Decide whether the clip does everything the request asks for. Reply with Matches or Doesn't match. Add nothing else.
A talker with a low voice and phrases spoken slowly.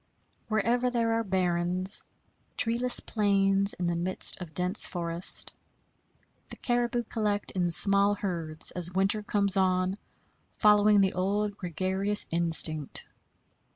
Doesn't match